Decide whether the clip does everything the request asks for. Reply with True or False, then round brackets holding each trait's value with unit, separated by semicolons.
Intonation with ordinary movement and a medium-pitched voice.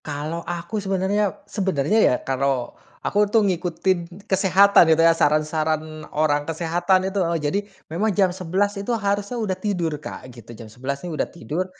True (4.2 semitones; 175 Hz)